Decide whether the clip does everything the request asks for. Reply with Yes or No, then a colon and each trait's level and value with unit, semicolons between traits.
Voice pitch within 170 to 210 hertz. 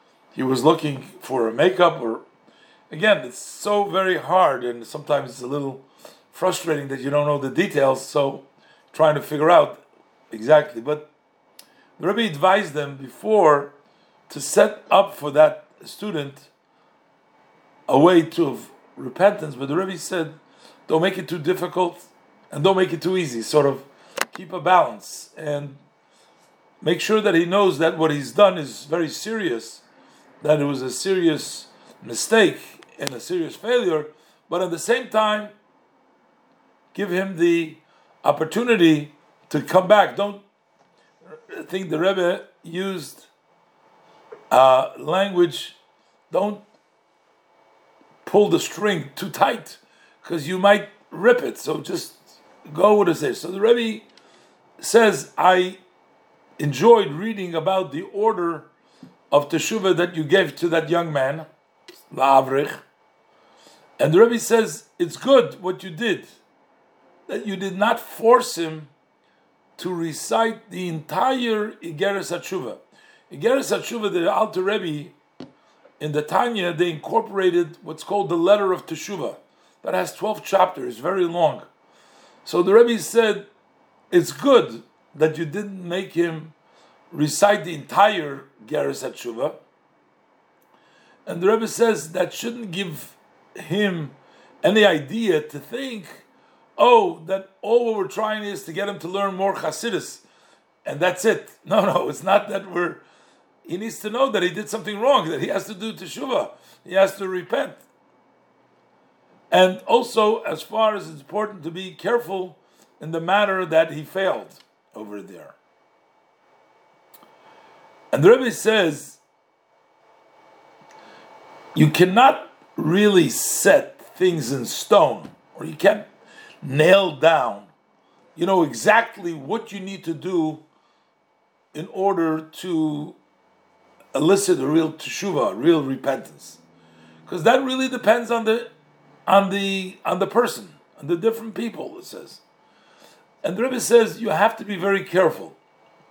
Yes: medium, 185 Hz